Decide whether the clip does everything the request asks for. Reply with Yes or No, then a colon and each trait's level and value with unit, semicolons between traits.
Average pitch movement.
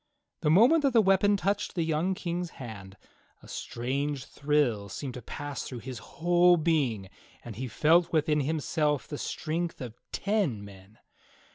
No: wide, 5.9 semitones